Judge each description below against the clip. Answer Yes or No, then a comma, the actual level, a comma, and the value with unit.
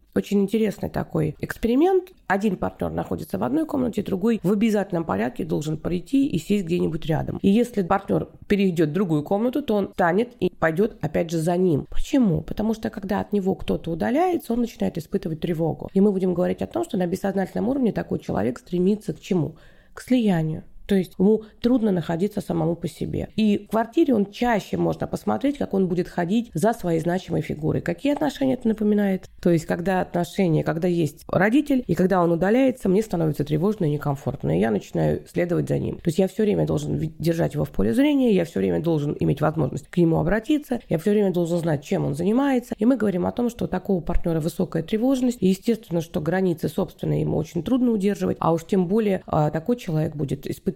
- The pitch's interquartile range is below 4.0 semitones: No, average, 4.7 semitones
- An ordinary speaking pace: No, fast, 200 wpm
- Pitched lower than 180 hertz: No, high, 190 Hz